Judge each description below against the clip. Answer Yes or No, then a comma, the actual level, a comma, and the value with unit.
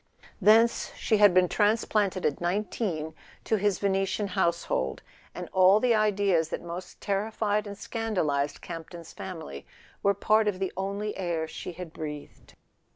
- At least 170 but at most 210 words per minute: No, average, 155 wpm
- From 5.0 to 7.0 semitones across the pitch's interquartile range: No, average, 3.6 semitones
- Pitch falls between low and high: No, high, 195 Hz